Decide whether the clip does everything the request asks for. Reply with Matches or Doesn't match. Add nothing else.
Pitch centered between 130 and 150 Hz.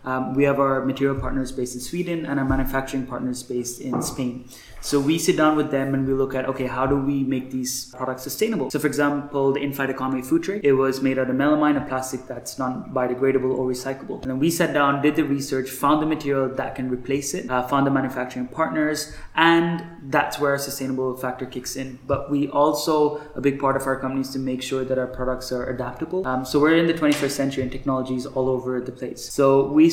Matches